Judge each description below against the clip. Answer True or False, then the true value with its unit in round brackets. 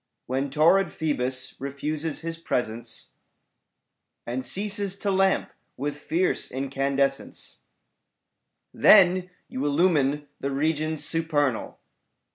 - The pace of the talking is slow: True (90 wpm)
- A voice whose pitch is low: False (145 Hz)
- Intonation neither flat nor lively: True (3.5 semitones)